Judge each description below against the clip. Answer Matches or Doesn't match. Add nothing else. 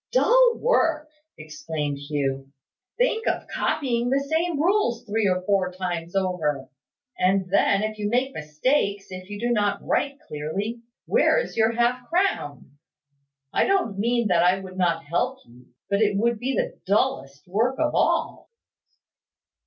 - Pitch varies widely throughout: Matches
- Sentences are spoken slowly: Doesn't match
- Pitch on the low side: Doesn't match